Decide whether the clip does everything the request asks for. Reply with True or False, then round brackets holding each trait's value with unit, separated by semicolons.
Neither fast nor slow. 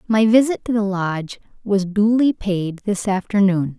True (160 wpm)